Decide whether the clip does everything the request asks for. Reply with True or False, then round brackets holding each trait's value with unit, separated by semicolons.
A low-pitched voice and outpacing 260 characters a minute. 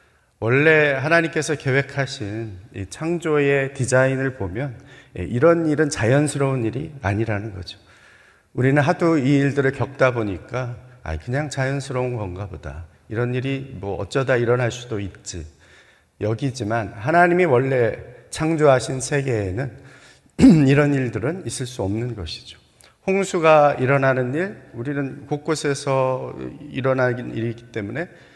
True (130 Hz; 285 characters per minute)